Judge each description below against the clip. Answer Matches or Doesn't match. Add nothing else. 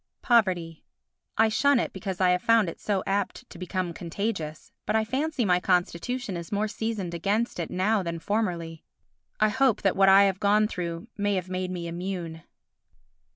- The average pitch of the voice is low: Doesn't match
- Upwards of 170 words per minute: Matches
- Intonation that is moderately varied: Matches